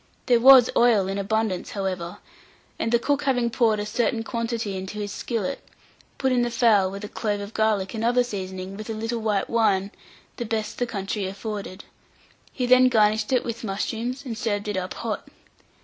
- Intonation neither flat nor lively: Yes, average, 3.0 semitones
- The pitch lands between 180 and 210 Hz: No, high, 220 Hz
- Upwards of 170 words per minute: Yes, average, 190 wpm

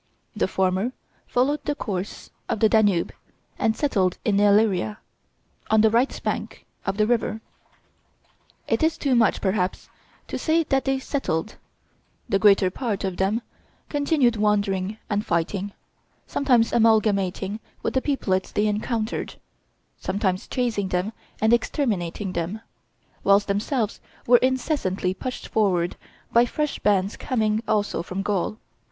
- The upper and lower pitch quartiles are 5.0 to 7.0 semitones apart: No, average, 3.8 semitones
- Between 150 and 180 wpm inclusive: No, slow, 135 wpm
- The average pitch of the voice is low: No, high, 210 Hz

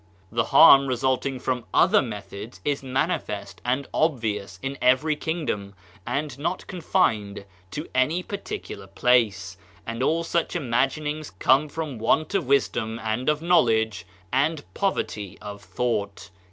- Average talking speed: No, slow, 130 wpm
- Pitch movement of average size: No, wide, 5.8 semitones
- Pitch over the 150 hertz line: No, low, 130 Hz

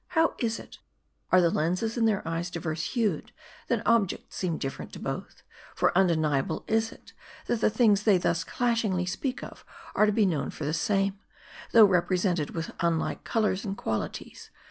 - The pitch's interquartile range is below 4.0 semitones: No, average, 4.7 semitones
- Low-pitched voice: No, high, 190 Hz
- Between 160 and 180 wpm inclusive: Yes, average, 175 wpm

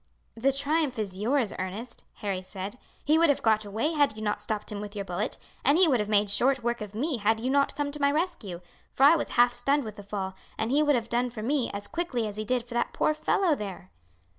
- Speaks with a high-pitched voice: Yes, high, 235 Hz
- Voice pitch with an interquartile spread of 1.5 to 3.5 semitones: No, average, 5.3 semitones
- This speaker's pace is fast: Yes, fast, 255 wpm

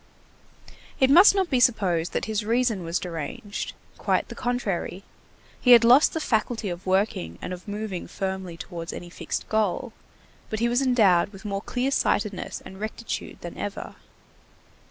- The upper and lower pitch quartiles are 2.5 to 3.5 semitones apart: No, average, 4.9 semitones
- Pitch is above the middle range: Yes, high, 205 Hz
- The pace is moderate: Yes, average, 160 wpm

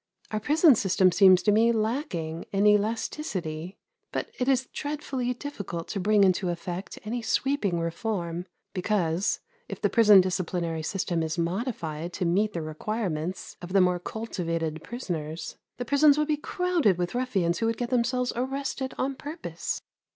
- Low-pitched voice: No, high, 200 Hz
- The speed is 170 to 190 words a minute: No, average, 155 wpm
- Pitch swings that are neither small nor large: No, wide, 6.2 semitones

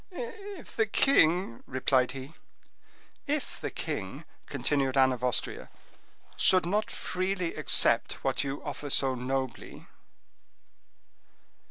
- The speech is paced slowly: Yes, slow, 110 wpm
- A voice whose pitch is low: No, medium, 145 Hz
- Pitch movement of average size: No, wide, 7.5 semitones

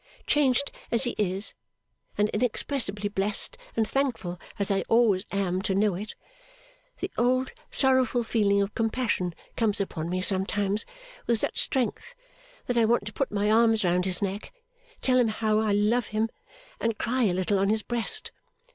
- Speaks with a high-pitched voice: Yes, high, 215 Hz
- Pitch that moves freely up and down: No, average, 3.2 semitones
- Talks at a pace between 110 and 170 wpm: Yes, average, 165 wpm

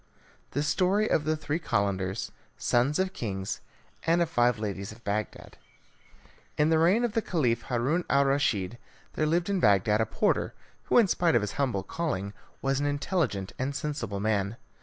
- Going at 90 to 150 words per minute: No, average, 175 wpm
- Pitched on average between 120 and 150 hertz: Yes, low, 135 Hz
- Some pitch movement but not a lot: No, wide, 7.6 semitones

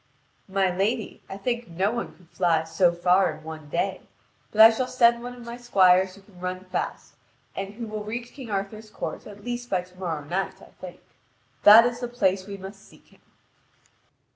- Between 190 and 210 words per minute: Yes, fast, 205 wpm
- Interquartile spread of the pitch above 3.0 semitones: Yes, average, 4.2 semitones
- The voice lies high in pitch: Yes, high, 195 Hz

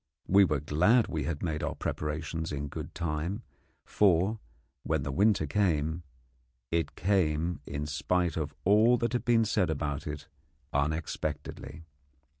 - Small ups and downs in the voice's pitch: No, average, 4.6 semitones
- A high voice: No, very low, 80 Hz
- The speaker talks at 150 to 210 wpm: No, average, 140 wpm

